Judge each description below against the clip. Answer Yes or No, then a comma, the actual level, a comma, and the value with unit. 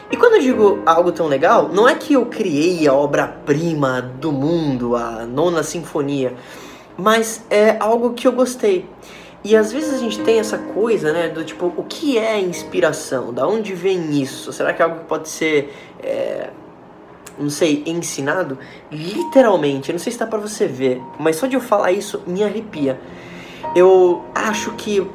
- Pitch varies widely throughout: Yes, wide, 7.1 semitones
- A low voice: No, medium, 175 Hz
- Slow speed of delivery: No, average, 180 wpm